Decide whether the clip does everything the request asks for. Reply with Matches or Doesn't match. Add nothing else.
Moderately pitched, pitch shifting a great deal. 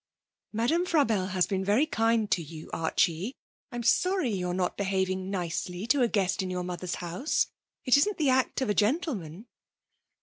Doesn't match